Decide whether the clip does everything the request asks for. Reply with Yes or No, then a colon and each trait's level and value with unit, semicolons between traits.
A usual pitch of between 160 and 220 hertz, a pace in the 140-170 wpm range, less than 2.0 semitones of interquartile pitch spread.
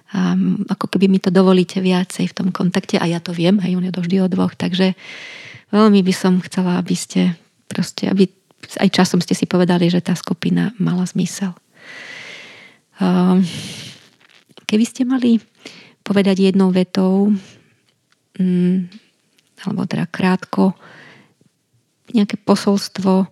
No: high, 190 Hz; average, 130 wpm; narrow, 1.6 semitones